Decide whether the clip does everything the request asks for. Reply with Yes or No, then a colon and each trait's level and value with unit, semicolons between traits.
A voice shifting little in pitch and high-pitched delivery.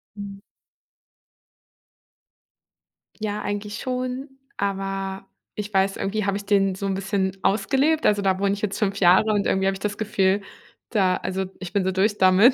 Yes: narrow, 1.5 semitones; high, 200 Hz